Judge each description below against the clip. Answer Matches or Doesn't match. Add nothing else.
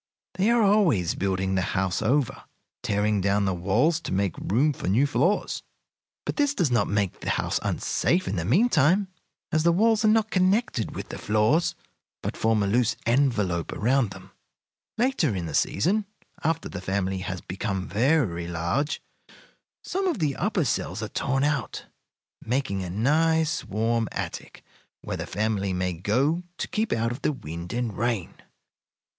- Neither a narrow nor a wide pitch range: Doesn't match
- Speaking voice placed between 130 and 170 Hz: Doesn't match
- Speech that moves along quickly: Doesn't match